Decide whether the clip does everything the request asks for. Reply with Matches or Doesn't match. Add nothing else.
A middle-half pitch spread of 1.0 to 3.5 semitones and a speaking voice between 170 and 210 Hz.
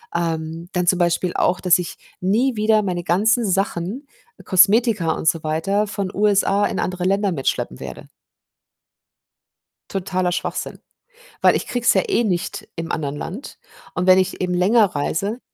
Matches